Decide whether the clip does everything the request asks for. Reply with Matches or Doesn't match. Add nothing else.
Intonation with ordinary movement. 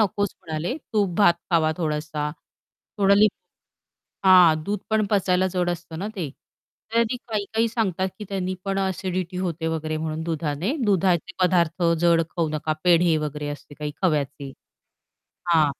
Matches